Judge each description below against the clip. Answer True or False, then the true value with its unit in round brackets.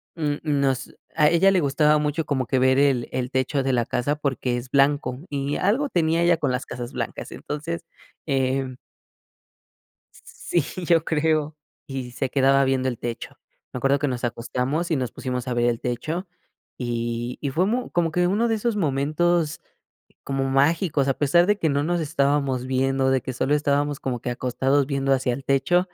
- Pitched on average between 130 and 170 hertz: True (140 Hz)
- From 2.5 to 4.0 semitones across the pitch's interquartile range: True (3.5 semitones)